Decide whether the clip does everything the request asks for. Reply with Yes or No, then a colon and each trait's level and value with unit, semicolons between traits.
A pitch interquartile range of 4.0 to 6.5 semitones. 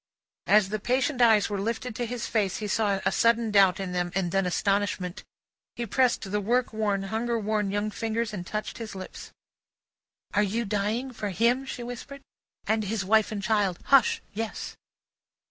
No: average, 2.8 semitones